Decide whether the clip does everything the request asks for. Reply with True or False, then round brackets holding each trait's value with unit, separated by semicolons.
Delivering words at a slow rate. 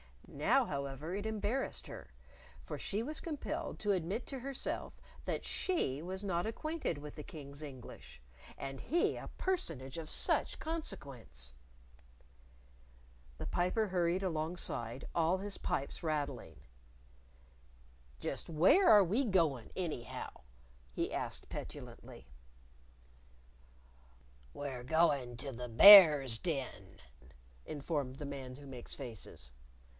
True (115 wpm)